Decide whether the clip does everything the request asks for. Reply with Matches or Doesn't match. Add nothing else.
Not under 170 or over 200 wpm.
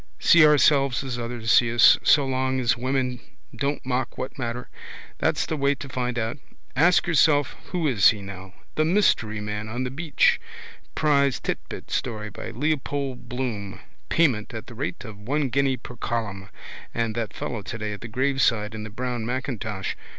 Matches